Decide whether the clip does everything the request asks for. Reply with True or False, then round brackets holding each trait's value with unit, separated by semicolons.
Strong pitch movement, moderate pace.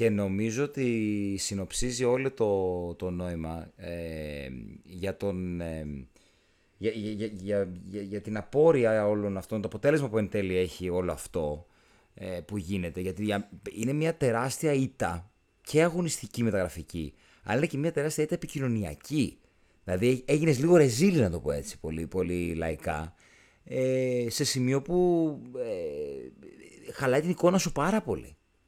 True (7.4 semitones; 140 wpm)